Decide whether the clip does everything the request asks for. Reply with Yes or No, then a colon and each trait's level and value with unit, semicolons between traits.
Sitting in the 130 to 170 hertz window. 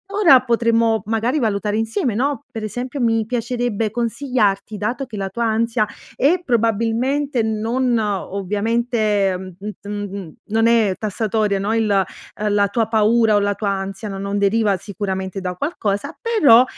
No: high, 220 Hz